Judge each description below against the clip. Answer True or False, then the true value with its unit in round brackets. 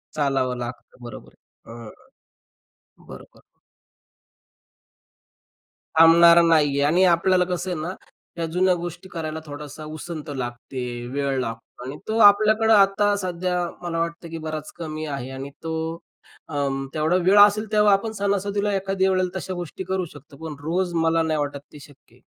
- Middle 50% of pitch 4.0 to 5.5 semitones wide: True (4.4 semitones)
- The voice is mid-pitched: True (165 Hz)